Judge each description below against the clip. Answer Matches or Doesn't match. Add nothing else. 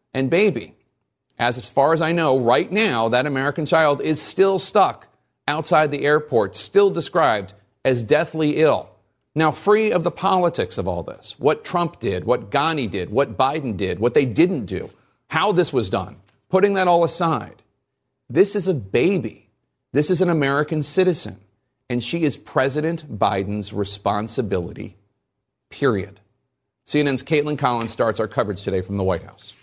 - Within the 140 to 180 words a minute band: Matches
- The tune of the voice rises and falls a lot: Matches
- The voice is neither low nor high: Matches